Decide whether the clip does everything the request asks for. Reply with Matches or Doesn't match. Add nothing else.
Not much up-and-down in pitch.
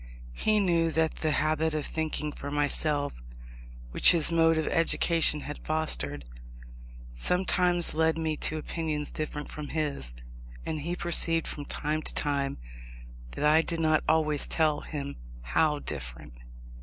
Matches